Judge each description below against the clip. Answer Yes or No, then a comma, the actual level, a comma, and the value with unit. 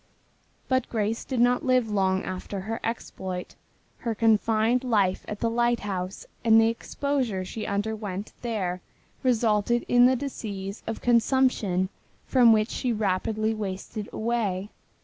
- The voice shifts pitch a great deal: No, average, 3.2 semitones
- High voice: Yes, high, 220 Hz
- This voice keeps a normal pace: No, slow, 130 wpm